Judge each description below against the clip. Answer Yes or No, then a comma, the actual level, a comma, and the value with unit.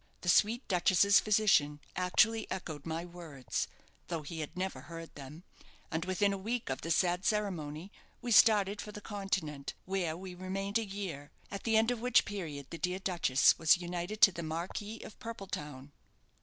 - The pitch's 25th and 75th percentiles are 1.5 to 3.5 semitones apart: No, average, 4.0 semitones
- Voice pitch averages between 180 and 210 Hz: Yes, medium, 185 Hz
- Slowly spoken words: No, average, 175 wpm